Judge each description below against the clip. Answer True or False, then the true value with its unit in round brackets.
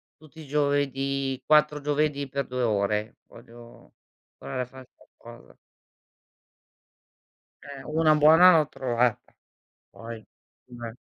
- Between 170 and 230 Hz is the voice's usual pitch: False (135 Hz)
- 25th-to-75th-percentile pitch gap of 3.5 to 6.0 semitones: True (4.0 semitones)